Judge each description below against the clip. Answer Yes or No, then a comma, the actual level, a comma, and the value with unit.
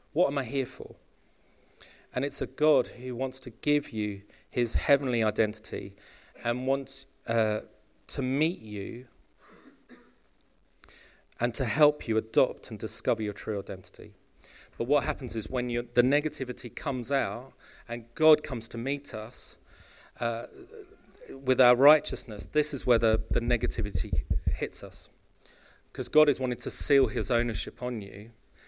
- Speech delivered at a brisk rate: No, average, 145 wpm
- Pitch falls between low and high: No, low, 125 Hz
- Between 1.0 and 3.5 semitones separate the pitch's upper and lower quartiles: Yes, average, 3.1 semitones